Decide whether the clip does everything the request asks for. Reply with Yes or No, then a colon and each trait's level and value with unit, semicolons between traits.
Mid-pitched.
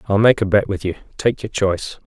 No: low, 100 Hz